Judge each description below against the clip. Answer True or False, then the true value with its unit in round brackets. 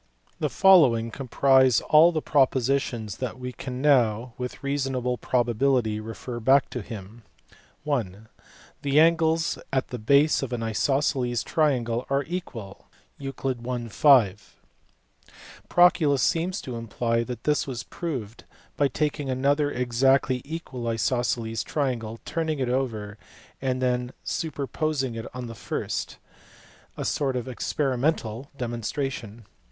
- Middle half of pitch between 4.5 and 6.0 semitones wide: False (3.2 semitones)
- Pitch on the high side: False (130 Hz)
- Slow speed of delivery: True (125 wpm)